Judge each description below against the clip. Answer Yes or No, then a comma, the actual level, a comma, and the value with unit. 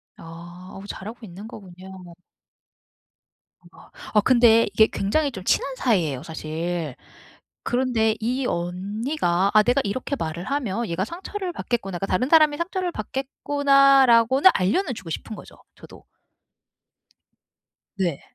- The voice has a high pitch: Yes, high, 220 Hz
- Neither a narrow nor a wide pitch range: No, wide, 6.6 semitones